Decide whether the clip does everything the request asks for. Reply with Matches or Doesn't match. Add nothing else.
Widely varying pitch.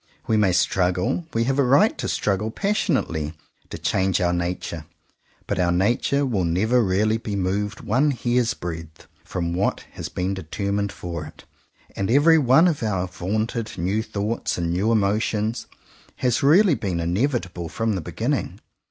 Doesn't match